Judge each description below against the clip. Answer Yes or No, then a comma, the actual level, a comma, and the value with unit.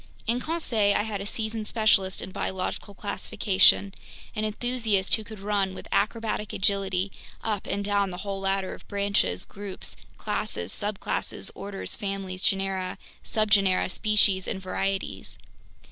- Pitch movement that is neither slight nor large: No, narrow, 1.8 semitones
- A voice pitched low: No, high, 200 Hz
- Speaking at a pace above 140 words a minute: No, slow, 135 wpm